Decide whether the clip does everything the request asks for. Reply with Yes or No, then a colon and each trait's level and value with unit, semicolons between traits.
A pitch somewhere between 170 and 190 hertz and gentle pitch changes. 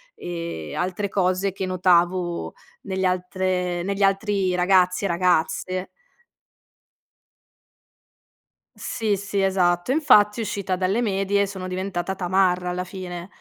Yes: medium, 185 Hz; narrow, 1.7 semitones